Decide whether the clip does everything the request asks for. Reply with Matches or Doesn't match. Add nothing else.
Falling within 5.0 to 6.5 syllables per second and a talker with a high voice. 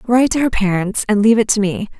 Doesn't match